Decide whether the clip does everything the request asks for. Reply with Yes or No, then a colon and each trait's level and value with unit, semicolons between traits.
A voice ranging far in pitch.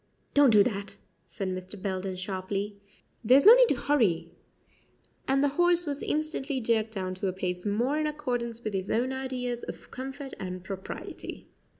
Yes: wide, 6.2 semitones